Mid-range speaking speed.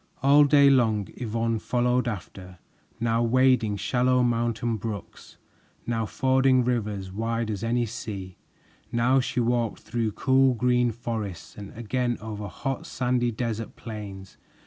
No: slow, 130 wpm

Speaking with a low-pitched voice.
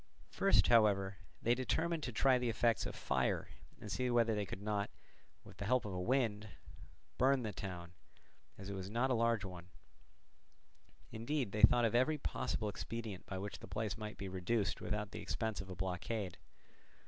Yes: low, 110 Hz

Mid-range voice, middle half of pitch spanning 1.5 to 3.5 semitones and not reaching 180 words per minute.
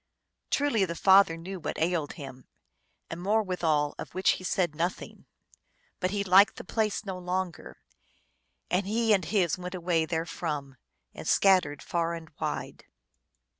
Yes: medium, 180 Hz; average, 2.9 semitones; average, 150 wpm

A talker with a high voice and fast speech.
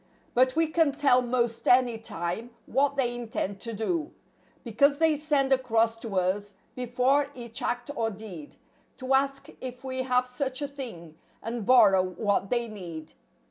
No: high, 245 Hz; average, 160 wpm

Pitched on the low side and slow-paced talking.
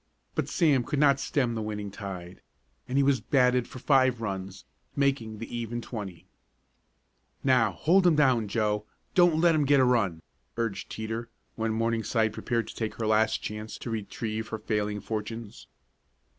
No: low, 115 Hz; average, 165 wpm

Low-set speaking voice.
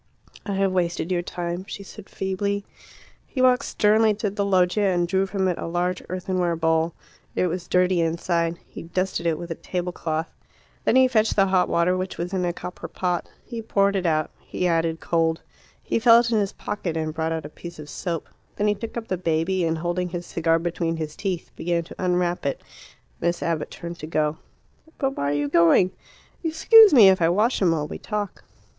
No: medium, 180 Hz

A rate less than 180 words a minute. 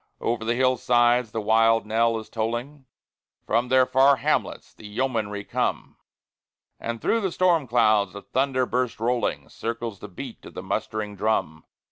Yes: average, 155 wpm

